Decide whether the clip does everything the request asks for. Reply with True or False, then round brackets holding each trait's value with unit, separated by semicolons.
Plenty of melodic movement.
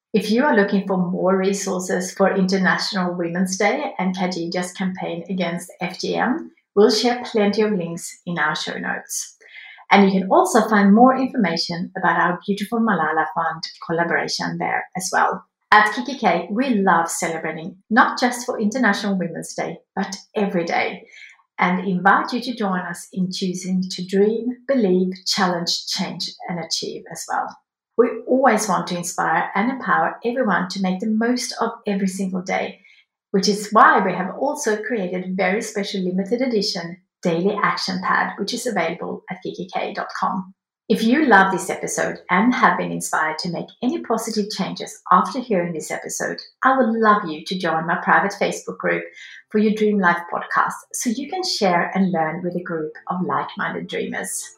False (3.9 semitones)